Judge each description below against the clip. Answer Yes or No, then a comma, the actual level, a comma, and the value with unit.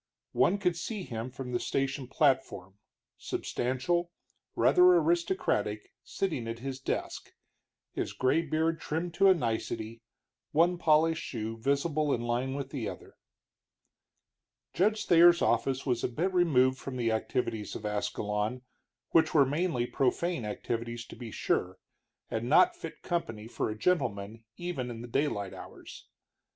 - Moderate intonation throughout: No, wide, 6.3 semitones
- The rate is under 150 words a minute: Yes, average, 140 wpm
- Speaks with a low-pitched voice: Yes, low, 130 Hz